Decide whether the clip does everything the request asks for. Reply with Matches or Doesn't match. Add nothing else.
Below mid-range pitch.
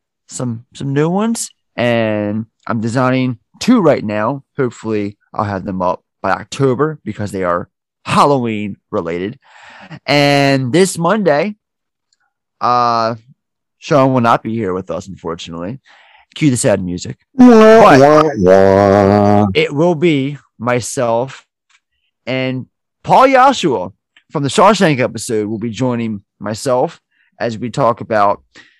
Matches